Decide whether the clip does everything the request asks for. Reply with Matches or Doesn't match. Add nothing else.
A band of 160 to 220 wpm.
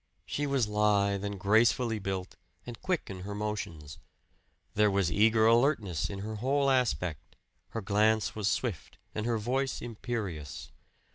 Doesn't match